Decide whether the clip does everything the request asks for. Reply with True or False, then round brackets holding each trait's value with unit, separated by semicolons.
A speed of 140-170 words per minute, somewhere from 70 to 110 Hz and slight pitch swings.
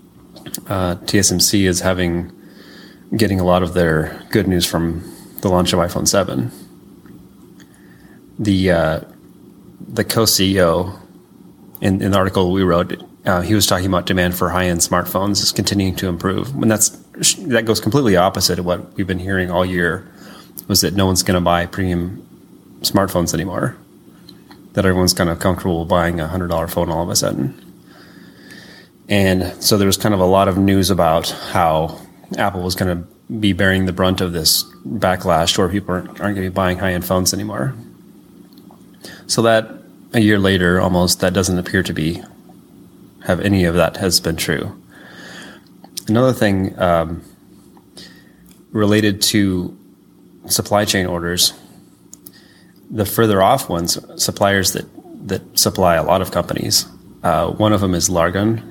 True (155 wpm; 95 Hz; 2.1 semitones)